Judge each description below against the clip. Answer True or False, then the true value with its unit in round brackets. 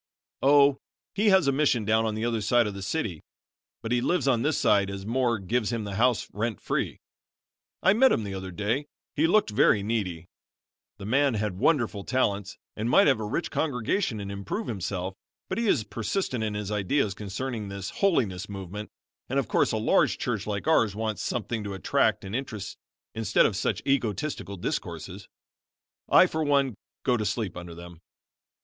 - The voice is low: True (110 Hz)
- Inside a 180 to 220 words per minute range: True (185 wpm)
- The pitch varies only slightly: False (5.0 semitones)